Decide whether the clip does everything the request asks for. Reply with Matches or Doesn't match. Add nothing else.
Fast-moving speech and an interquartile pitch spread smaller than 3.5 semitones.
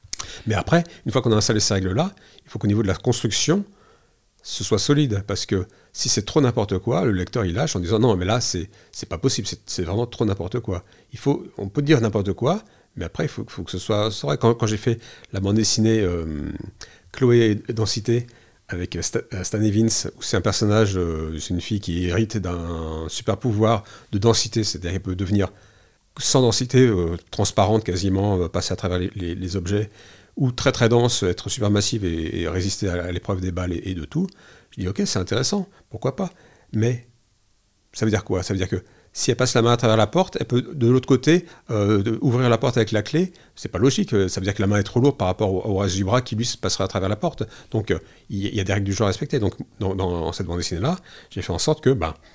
Doesn't match